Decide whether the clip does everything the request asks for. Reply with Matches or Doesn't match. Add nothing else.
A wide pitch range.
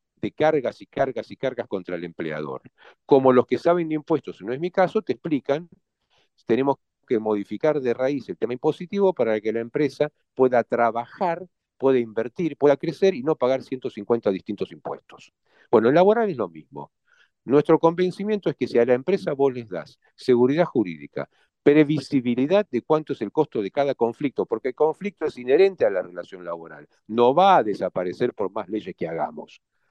Matches